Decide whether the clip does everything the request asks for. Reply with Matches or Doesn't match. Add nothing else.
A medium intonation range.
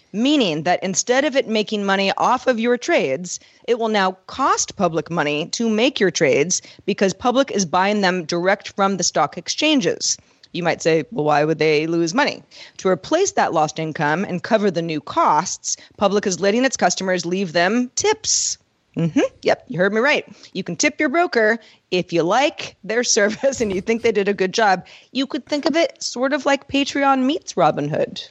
Doesn't match